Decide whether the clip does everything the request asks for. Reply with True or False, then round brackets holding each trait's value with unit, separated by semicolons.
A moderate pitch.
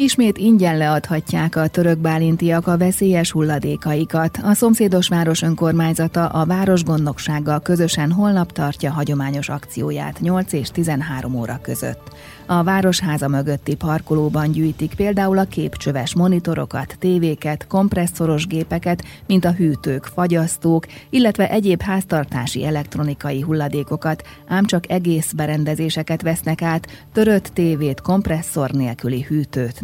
True (160 Hz)